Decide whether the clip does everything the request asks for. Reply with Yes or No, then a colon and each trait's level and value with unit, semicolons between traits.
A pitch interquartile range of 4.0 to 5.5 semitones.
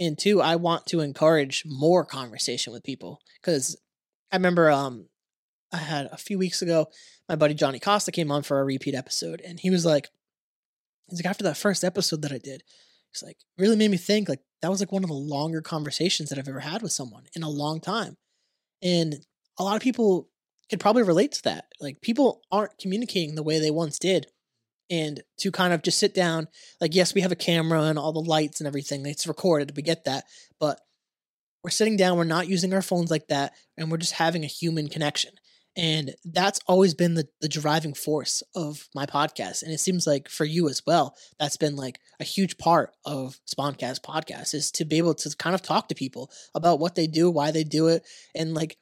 No: average, 3.6 semitones